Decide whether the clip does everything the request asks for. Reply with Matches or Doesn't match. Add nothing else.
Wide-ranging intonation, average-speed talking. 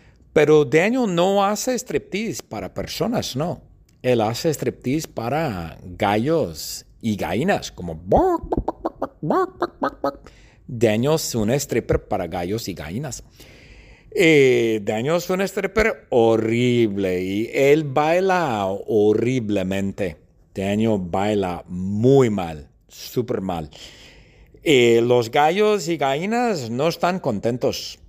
Doesn't match